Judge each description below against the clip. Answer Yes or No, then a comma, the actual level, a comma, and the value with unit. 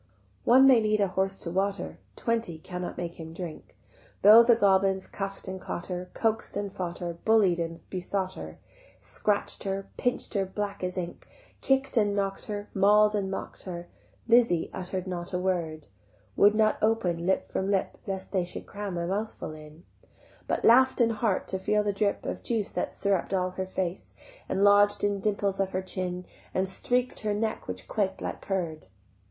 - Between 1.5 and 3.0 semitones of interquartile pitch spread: Yes, narrow, 2.5 semitones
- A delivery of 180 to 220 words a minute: Yes, average, 185 wpm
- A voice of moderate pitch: No, high, 195 Hz